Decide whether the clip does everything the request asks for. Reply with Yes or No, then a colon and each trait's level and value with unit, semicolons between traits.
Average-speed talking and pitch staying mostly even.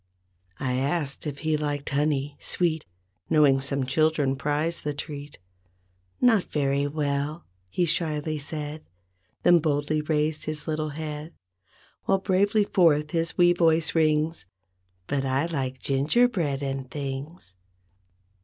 No: slow, 125 wpm; narrow, 2.3 semitones